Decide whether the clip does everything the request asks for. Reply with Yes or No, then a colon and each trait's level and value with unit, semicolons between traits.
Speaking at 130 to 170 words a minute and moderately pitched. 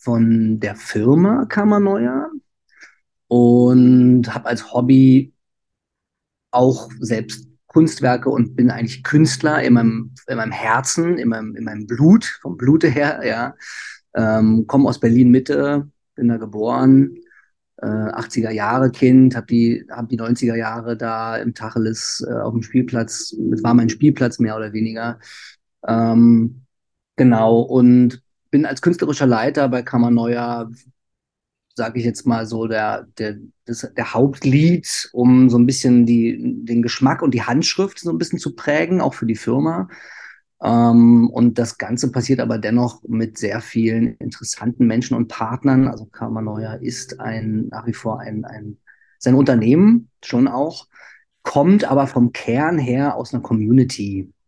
No: average, 150 wpm; low, 120 Hz